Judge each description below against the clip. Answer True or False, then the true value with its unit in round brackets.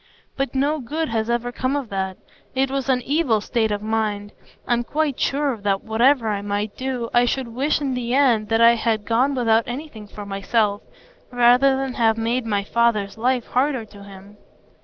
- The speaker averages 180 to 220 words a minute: True (190 wpm)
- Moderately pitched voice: False (235 Hz)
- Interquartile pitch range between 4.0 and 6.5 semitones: False (3.6 semitones)